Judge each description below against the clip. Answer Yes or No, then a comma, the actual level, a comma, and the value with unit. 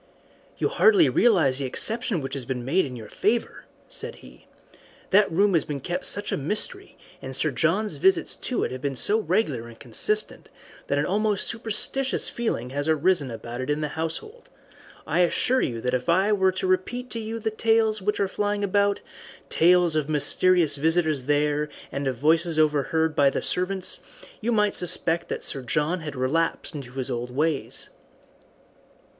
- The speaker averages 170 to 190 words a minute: Yes, average, 180 wpm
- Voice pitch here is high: No, medium, 165 Hz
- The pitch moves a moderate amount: No, wide, 6.6 semitones